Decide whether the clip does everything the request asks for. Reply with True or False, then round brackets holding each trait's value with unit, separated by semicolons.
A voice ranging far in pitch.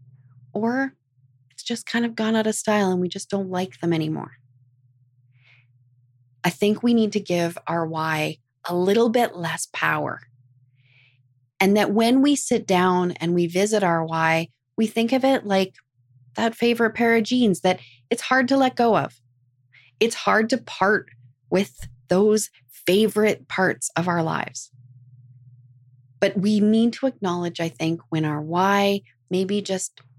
True (8.9 semitones)